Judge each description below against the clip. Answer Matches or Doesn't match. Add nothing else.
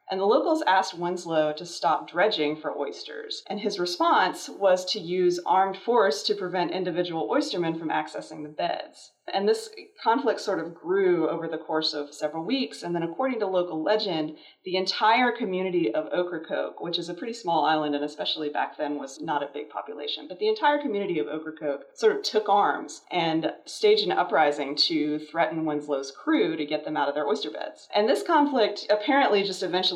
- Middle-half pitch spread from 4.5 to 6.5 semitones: Matches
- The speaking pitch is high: Doesn't match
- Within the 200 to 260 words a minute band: Doesn't match